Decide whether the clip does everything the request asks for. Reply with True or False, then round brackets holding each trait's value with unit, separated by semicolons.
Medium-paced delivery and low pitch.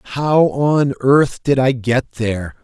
True (160 wpm; 130 Hz)